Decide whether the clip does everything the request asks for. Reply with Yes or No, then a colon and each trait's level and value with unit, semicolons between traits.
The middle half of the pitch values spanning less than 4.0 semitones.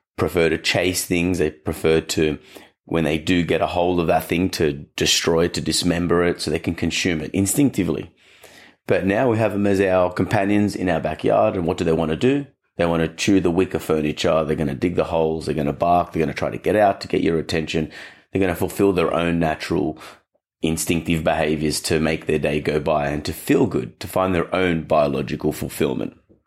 Yes: average, 2.8 semitones